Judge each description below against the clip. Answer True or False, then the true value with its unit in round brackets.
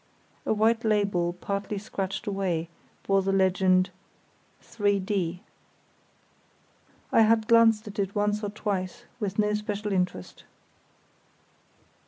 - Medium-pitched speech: False (200 Hz)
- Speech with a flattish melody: True (2.0 semitones)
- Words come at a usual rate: False (110 wpm)